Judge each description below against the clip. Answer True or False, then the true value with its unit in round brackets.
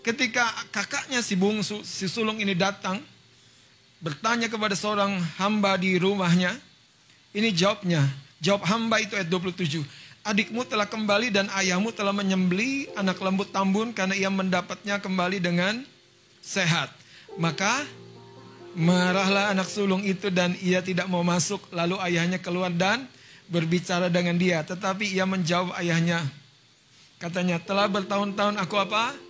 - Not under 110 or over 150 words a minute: True (130 wpm)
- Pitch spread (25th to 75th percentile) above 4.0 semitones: False (2.5 semitones)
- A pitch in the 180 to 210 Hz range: True (190 Hz)